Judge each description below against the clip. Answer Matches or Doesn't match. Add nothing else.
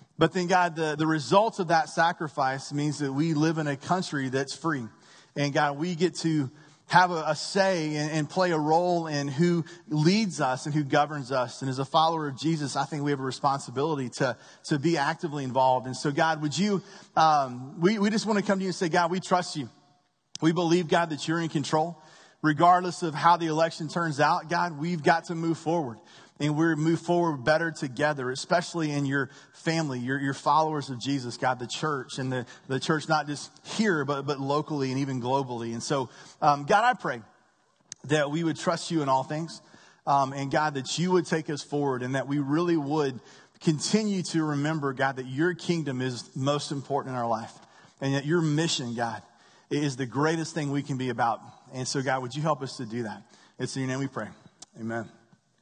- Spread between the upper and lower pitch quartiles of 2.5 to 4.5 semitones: Matches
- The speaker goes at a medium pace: Doesn't match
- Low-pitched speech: Doesn't match